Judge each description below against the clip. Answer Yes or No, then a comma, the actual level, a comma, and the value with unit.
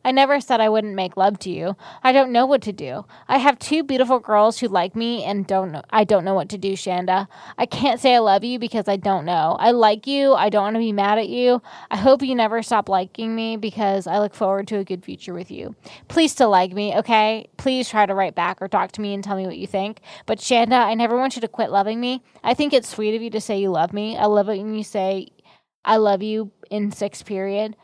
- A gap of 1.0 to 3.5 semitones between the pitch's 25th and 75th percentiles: Yes, average, 3.2 semitones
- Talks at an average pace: No, fast, 265 wpm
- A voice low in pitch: No, high, 215 Hz